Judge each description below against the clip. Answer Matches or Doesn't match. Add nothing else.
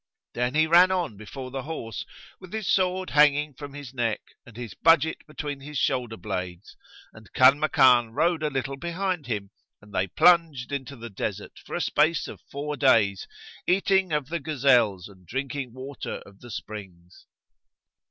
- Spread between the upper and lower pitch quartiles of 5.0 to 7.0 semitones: Matches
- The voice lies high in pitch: Doesn't match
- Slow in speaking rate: Doesn't match